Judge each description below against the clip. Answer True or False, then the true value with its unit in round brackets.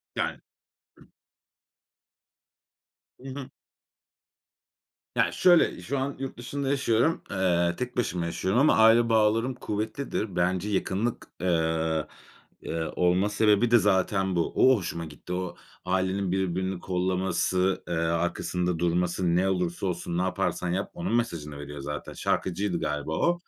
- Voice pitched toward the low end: True (95 Hz)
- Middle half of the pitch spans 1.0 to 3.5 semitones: False (4.3 semitones)